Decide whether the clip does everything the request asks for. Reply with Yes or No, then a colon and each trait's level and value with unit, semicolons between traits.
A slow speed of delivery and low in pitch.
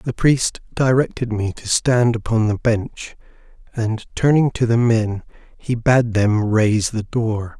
No: average, 160 wpm; low, 115 Hz